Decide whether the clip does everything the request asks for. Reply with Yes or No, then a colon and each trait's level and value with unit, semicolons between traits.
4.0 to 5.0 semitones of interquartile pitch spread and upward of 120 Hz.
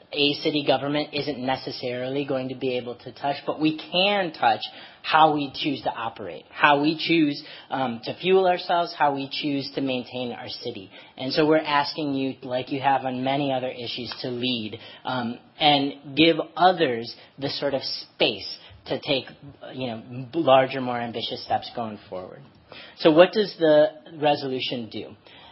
No: average, 3.4 semitones; medium, 140 Hz